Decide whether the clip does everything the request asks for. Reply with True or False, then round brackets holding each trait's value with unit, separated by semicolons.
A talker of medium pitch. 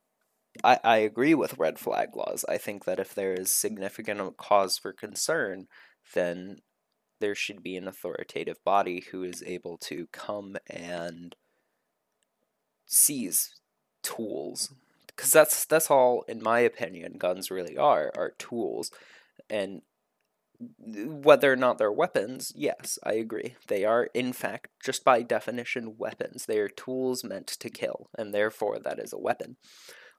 False (110 Hz)